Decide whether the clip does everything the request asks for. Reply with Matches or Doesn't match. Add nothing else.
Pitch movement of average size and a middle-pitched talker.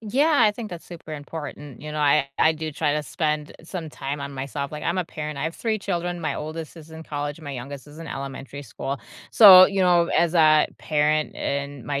Matches